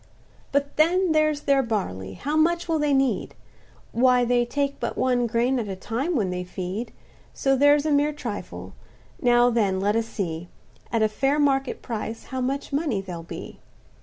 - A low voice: No, very high, 250 Hz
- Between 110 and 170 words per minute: No, average, 180 wpm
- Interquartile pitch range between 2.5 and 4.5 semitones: No, average, 4.9 semitones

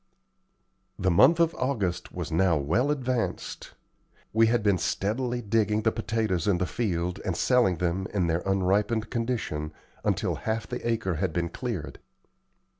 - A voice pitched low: Yes, low, 105 Hz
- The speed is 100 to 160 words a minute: Yes, average, 150 wpm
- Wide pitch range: No, average, 4.6 semitones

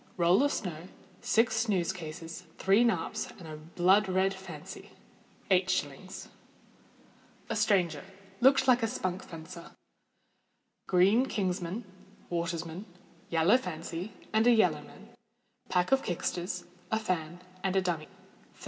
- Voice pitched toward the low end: No, medium, 185 Hz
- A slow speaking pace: Yes, slow, 125 wpm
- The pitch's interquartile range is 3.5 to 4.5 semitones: Yes, average, 3.8 semitones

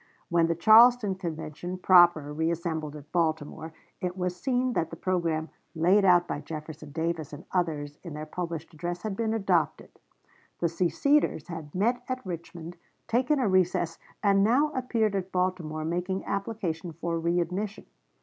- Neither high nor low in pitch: Yes, medium, 175 Hz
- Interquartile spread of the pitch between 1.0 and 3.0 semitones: No, average, 3.4 semitones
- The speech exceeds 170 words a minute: No, average, 150 wpm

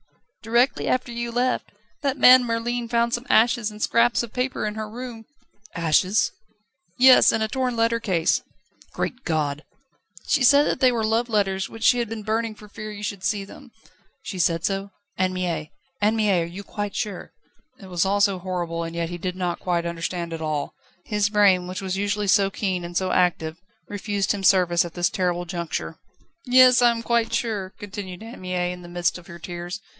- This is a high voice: Yes, high, 200 Hz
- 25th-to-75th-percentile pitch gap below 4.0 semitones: No, average, 4.4 semitones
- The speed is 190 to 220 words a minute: Yes, average, 200 wpm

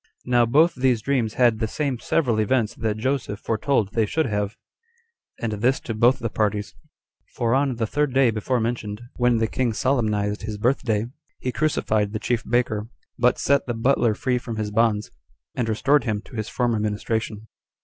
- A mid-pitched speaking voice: No, low, 115 Hz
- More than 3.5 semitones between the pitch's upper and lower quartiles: No, average, 2.9 semitones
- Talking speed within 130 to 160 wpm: No, average, 185 wpm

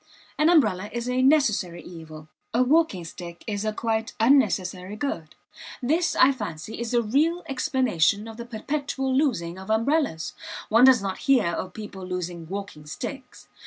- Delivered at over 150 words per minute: Yes, average, 160 wpm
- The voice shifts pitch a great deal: Yes, wide, 6.5 semitones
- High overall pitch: Yes, high, 220 Hz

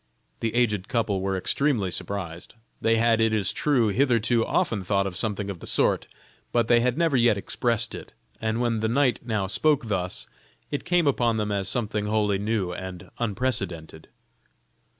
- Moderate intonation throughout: Yes, average, 3.4 semitones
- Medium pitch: No, low, 110 Hz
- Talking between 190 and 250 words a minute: No, average, 170 wpm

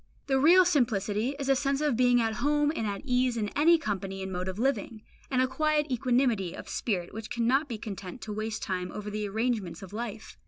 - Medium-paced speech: No, fast, 220 wpm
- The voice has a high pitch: Yes, high, 230 Hz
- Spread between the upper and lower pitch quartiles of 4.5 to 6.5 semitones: Yes, average, 4.8 semitones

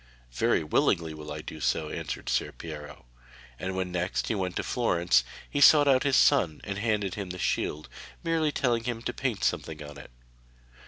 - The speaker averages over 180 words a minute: Yes, average, 190 wpm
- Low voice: Yes, very low, 95 Hz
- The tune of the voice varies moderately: No, wide, 7.5 semitones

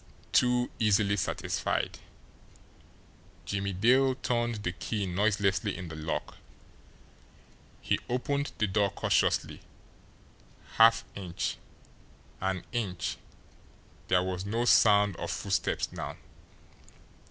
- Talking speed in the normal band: No, slow, 95 wpm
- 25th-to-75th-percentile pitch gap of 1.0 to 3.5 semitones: No, average, 3.9 semitones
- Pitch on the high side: No, low, 105 Hz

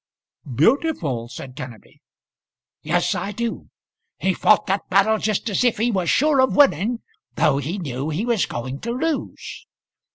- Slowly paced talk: No, average, 155 wpm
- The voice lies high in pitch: Yes, high, 200 Hz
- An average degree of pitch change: No, wide, 8.5 semitones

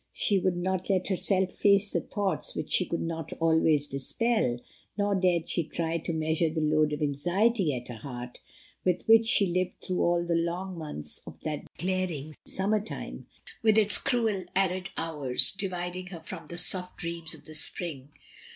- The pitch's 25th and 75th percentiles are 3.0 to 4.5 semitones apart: Yes, average, 3.4 semitones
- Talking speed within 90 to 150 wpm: No, average, 180 wpm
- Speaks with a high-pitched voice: No, medium, 175 Hz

